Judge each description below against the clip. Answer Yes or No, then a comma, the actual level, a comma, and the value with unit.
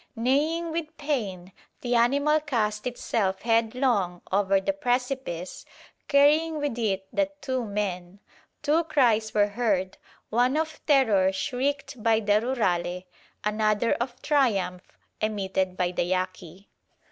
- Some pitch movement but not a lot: No, wide, 6.2 semitones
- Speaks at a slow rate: Yes, slow, 125 wpm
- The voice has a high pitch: Yes, high, 225 Hz